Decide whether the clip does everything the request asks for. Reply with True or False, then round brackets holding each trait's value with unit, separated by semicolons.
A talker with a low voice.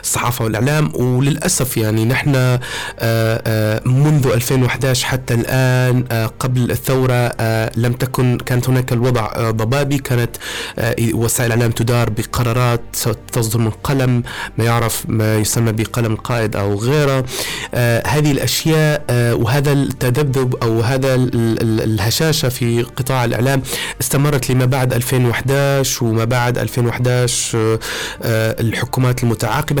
True (120 Hz)